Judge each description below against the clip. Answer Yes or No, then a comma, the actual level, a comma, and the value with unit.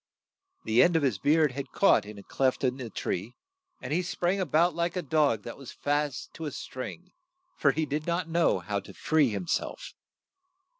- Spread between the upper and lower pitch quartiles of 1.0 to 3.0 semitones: No, average, 5.0 semitones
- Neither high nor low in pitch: Yes, medium, 150 Hz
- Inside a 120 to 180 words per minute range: No, fast, 205 wpm